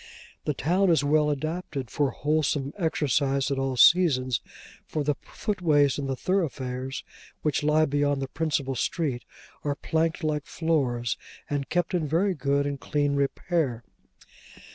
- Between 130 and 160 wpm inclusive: Yes, average, 140 wpm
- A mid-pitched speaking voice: Yes, medium, 145 Hz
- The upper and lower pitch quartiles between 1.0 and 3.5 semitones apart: Yes, average, 2.9 semitones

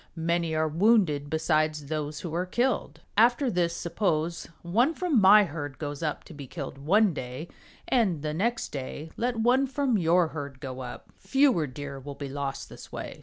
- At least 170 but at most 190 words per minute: Yes, average, 180 wpm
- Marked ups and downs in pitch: Yes, wide, 6.6 semitones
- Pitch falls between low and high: Yes, medium, 165 Hz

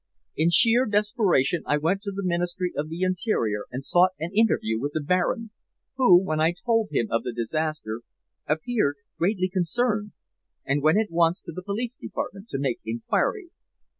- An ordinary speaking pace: Yes, average, 170 wpm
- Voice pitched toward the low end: No, medium, 175 Hz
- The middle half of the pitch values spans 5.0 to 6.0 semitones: Yes, wide, 5.6 semitones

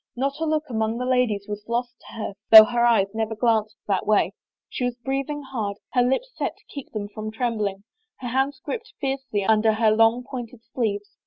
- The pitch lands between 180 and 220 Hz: No, high, 235 Hz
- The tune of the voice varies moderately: Yes, average, 3.3 semitones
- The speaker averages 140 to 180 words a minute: No, average, 200 wpm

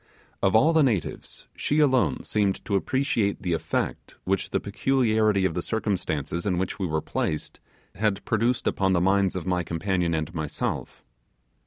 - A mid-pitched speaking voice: No, very low, 95 Hz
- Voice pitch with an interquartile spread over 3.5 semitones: Yes, average, 3.9 semitones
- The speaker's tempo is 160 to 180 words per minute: Yes, average, 165 wpm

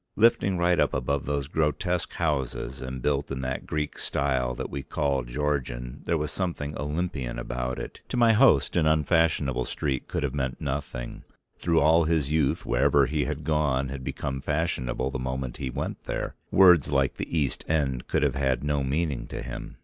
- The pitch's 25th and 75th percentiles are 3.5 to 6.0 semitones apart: No, average, 3.0 semitones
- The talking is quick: No, average, 185 wpm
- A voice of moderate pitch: No, very low, 70 Hz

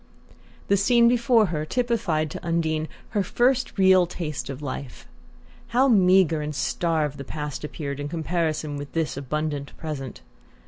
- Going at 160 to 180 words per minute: No, average, 145 wpm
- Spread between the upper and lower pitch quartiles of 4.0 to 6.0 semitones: Yes, average, 4.5 semitones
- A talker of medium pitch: Yes, medium, 160 Hz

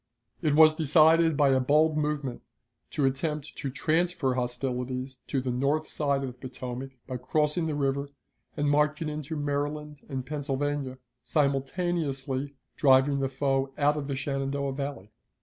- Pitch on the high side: No, medium, 140 Hz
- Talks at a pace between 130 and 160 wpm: Yes, average, 150 wpm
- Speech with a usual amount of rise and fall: No, narrow, 2.1 semitones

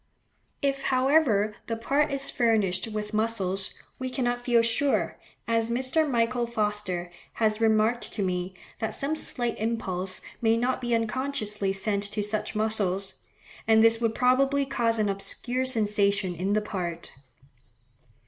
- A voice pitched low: No, high, 225 Hz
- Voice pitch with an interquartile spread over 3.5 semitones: No, average, 3.2 semitones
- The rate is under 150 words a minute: Yes, average, 140 wpm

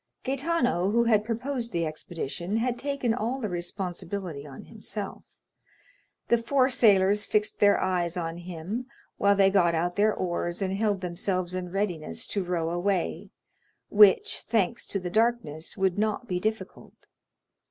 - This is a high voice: Yes, high, 195 Hz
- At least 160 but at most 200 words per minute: No, average, 150 wpm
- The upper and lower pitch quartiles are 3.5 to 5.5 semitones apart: Yes, average, 4.3 semitones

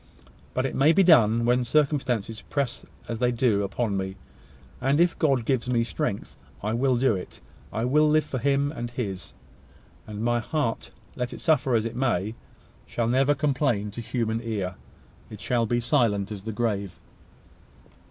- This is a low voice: Yes, low, 120 Hz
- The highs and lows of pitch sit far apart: No, average, 3.5 semitones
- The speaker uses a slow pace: No, average, 175 wpm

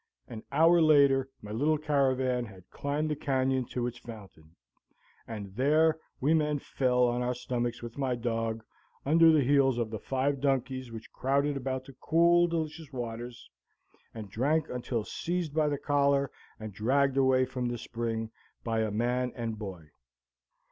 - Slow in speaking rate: No, average, 160 wpm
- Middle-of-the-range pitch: No, low, 130 Hz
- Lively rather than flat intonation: No, average, 3.6 semitones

